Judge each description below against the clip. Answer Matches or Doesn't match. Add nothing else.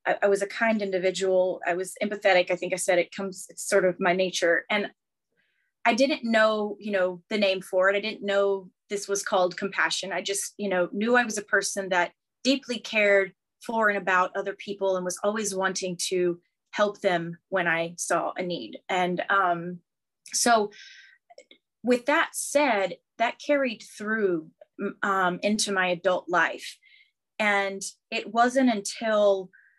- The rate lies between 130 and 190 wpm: Matches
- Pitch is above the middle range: Matches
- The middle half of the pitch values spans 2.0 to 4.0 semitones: Matches